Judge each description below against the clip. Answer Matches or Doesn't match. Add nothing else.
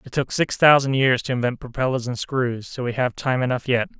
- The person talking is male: Matches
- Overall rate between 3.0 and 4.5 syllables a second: Doesn't match